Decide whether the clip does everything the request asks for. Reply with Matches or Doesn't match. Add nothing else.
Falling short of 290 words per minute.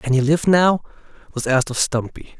Matches